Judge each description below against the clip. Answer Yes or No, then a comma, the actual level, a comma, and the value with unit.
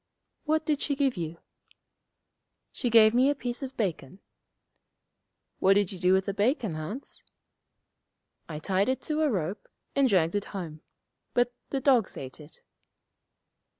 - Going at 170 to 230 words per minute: No, average, 150 wpm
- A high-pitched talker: Yes, high, 210 Hz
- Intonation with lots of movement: Yes, wide, 6.5 semitones